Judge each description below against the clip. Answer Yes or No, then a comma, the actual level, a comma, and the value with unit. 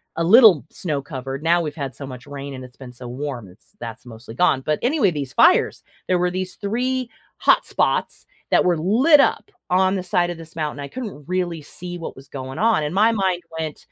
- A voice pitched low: No, medium, 165 Hz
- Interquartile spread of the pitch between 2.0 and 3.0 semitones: No, wide, 5.4 semitones